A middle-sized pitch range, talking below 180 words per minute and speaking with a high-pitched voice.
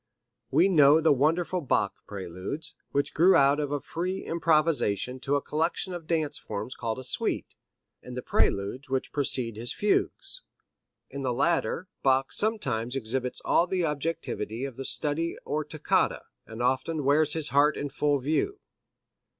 No: average, 4.2 semitones; average, 160 wpm; medium, 145 Hz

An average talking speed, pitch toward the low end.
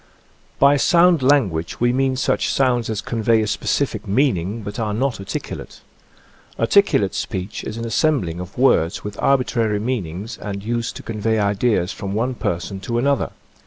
Yes: average, 160 wpm; low, 115 Hz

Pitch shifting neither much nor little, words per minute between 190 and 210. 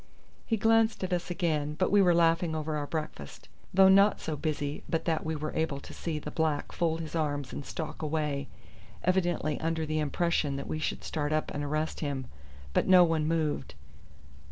No: narrow, 2.3 semitones; average, 195 wpm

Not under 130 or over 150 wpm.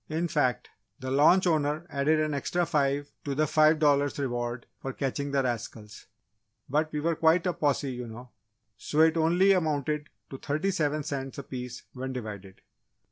No: average, 175 wpm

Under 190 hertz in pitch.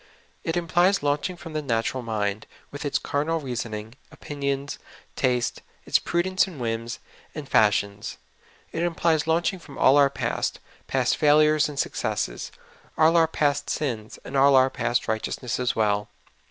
Yes: medium, 140 Hz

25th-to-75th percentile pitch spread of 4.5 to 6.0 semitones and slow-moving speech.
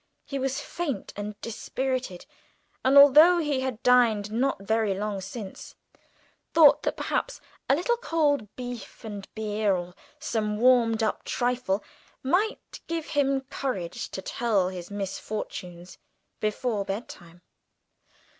Yes: average, 4.9 semitones; slow, 125 wpm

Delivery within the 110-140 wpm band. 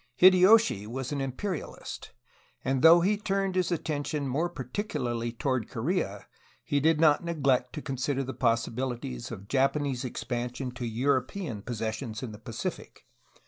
Yes: slow, 135 wpm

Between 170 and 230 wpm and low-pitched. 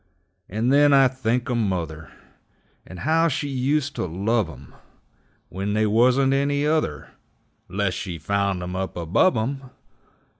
No: average, 145 wpm; low, 110 Hz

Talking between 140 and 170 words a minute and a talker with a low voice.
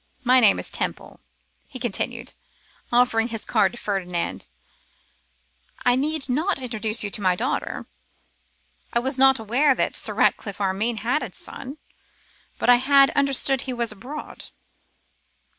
No: average, 145 wpm; high, 245 Hz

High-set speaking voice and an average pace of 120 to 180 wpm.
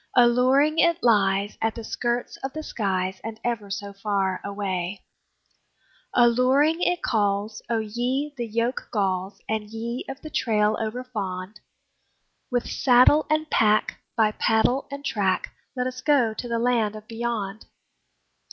Yes: high, 225 Hz; average, 140 wpm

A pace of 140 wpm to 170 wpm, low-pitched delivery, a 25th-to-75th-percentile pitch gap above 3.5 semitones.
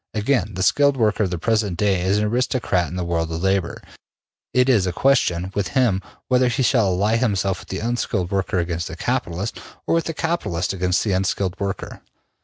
No: fast, 205 wpm; low, 100 Hz; average, 4.5 semitones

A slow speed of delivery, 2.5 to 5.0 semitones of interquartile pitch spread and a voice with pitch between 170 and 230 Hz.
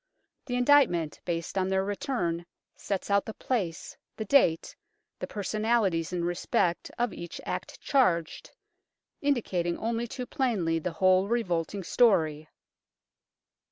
No: slow, 120 wpm; wide, 5.6 semitones; high, 190 Hz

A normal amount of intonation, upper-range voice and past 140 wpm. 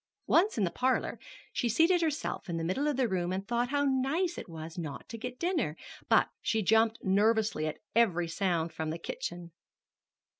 No: wide, 7.5 semitones; high, 220 Hz; average, 190 wpm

